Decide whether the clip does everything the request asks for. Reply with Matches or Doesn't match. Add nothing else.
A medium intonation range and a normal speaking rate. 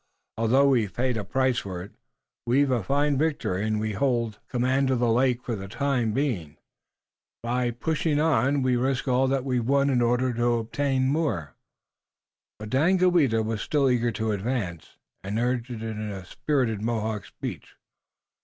Matches